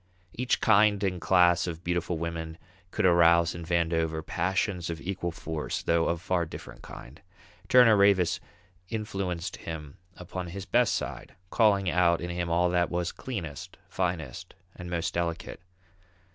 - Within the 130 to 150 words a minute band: Yes, average, 145 wpm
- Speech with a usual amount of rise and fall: No, narrow, 2.0 semitones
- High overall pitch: No, very low, 85 Hz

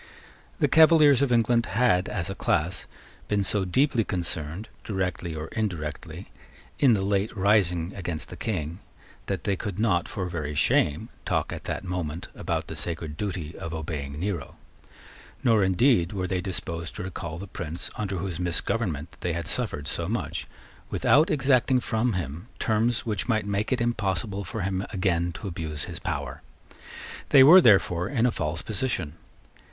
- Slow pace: No, average, 165 wpm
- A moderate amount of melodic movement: Yes, average, 4.7 semitones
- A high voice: No, very low, 95 Hz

